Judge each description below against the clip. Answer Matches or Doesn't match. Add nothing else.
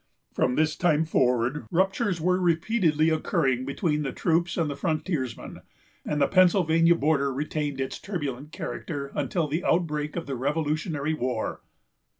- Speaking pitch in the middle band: Matches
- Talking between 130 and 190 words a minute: Matches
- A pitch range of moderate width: Matches